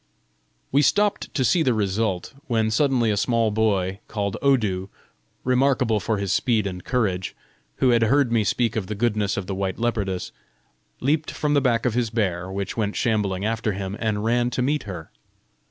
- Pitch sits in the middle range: No, low, 110 Hz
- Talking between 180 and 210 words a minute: Yes, average, 185 wpm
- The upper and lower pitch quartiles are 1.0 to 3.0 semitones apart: No, average, 3.8 semitones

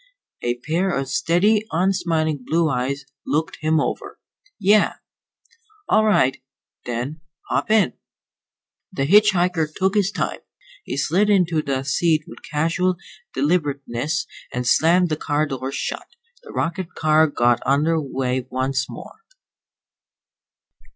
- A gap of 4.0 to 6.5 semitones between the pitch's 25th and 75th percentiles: Yes, average, 4.6 semitones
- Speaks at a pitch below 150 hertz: No, medium, 155 Hz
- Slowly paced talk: Yes, slow, 125 wpm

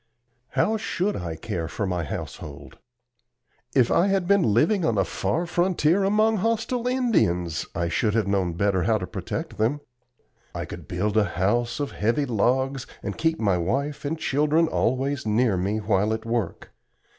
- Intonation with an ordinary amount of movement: No, wide, 8.8 semitones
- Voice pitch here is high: No, low, 120 Hz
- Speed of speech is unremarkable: Yes, average, 170 wpm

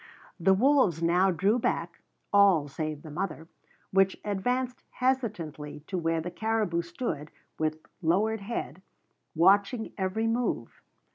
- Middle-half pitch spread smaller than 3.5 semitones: No, average, 5.2 semitones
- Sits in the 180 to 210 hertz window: Yes, high, 190 Hz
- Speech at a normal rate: No, slow, 125 wpm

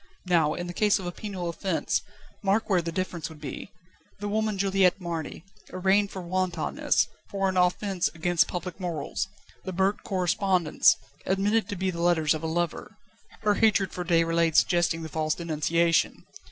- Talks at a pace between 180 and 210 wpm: No, average, 165 wpm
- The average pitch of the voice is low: No, medium, 180 Hz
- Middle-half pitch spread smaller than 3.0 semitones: Yes, narrow, 2.6 semitones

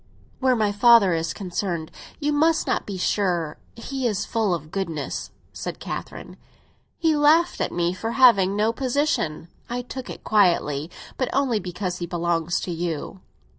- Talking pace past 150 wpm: Yes, average, 160 wpm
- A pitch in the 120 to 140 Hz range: No, high, 200 Hz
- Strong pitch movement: Yes, wide, 6.4 semitones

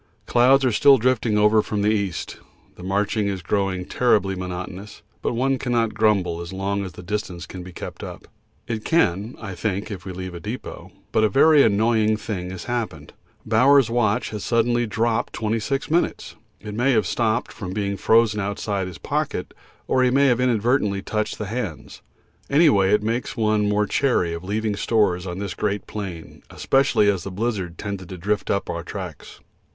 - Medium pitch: No, low, 105 Hz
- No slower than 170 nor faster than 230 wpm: Yes, average, 185 wpm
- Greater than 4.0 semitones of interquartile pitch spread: No, average, 3.5 semitones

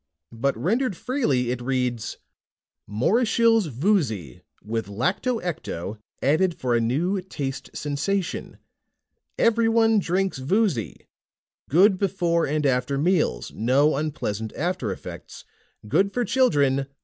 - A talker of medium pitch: Yes, medium, 150 Hz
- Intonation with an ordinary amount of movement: No, wide, 7.8 semitones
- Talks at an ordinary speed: No, slow, 110 wpm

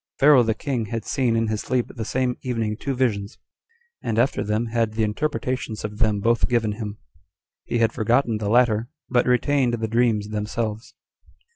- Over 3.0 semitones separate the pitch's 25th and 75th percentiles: No, narrow, 2.4 semitones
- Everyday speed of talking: Yes, average, 175 wpm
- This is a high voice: No, low, 115 Hz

